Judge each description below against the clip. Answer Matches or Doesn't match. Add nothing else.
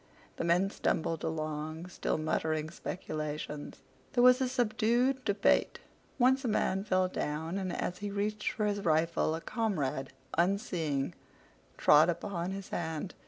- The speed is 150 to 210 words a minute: Doesn't match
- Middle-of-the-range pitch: Matches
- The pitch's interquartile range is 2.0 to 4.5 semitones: Doesn't match